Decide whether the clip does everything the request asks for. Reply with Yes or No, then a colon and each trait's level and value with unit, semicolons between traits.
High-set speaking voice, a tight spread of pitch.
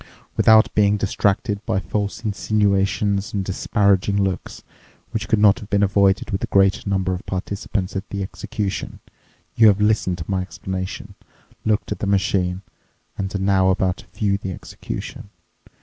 No: low, 100 Hz; narrow, 1.4 semitones